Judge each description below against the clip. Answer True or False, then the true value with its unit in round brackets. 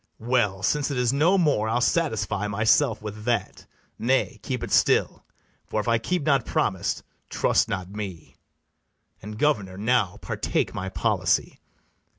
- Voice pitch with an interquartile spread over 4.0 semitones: True (4.7 semitones)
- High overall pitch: False (115 Hz)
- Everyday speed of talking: True (150 wpm)